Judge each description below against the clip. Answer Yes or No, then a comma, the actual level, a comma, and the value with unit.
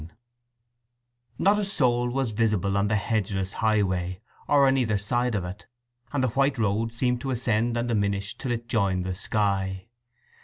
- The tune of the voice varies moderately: Yes, average, 3.7 semitones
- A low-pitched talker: Yes, low, 110 Hz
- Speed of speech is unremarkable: Yes, average, 170 wpm